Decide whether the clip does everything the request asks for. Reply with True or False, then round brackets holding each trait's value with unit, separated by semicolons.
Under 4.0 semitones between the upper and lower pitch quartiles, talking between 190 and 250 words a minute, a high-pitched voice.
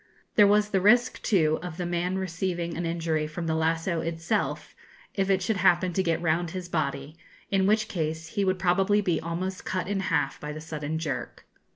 False (2.9 semitones; 200 wpm; 175 Hz)